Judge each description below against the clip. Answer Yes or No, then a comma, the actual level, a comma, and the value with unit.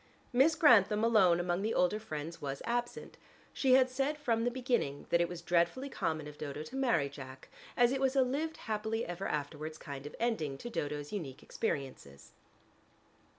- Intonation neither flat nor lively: No, wide, 8.5 semitones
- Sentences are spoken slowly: No, average, 180 wpm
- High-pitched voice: Yes, high, 195 Hz